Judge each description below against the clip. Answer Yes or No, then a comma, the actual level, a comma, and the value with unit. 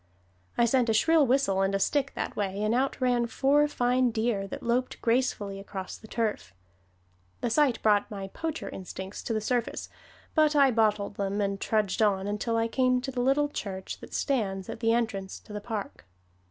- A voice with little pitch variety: No, average, 4.2 semitones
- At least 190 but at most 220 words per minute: Yes, average, 195 wpm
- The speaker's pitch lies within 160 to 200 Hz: No, high, 225 Hz